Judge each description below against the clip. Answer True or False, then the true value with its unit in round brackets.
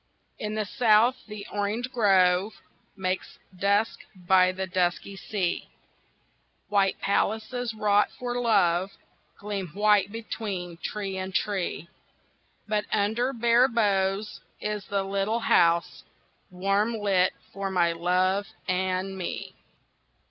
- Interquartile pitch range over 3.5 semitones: False (2.4 semitones)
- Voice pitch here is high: True (200 Hz)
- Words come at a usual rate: False (110 wpm)